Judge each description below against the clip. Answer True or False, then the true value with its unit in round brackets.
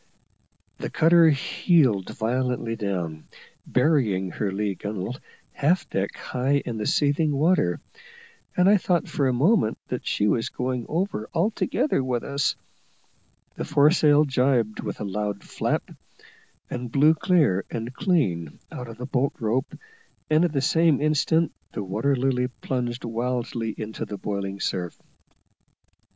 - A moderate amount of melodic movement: False (6.0 semitones)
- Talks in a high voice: False (125 Hz)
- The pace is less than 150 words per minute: True (140 wpm)